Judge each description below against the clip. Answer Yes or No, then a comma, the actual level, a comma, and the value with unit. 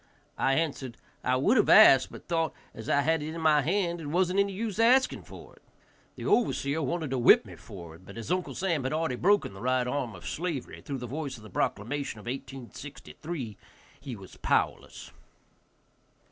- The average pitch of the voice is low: No, medium, 145 Hz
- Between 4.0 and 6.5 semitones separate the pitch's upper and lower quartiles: Yes, wide, 5.4 semitones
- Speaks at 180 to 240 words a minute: Yes, average, 190 wpm